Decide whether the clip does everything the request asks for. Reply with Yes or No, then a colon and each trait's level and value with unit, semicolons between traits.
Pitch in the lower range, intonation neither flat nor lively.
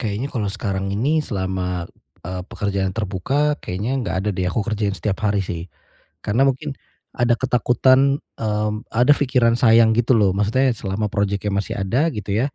Yes: low, 105 Hz; average, 4.1 semitones